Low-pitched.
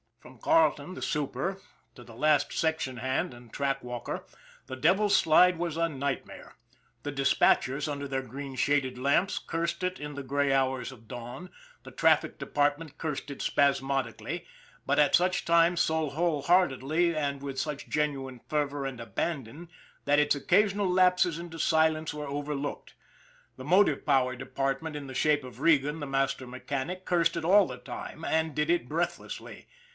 No: medium, 145 Hz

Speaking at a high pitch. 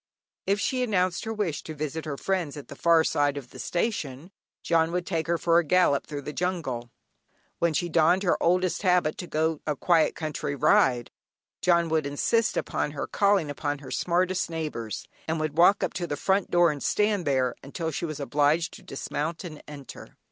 No: medium, 160 Hz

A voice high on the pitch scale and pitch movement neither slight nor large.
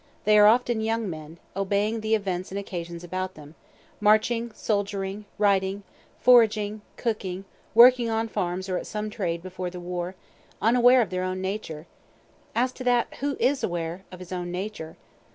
Yes: high, 200 Hz; average, 3.5 semitones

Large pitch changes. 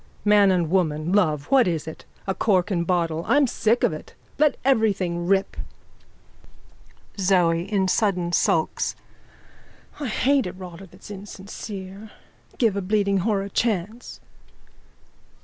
No: average, 3.4 semitones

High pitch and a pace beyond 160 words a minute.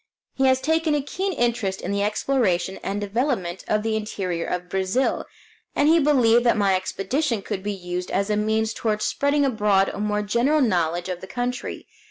Yes: high, 215 Hz; average, 190 wpm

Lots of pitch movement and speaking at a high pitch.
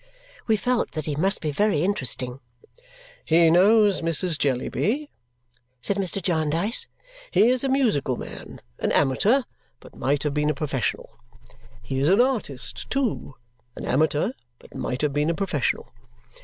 No: wide, 6.5 semitones; medium, 165 Hz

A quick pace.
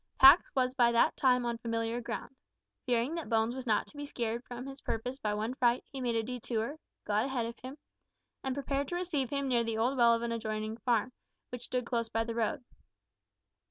Yes: fast, 215 wpm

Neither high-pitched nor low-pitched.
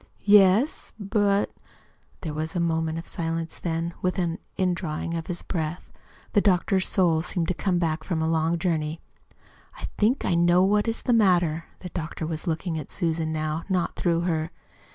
Yes: medium, 170 Hz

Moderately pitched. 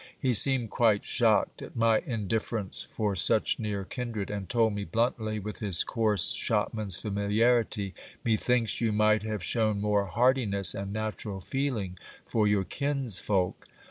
No: low, 110 Hz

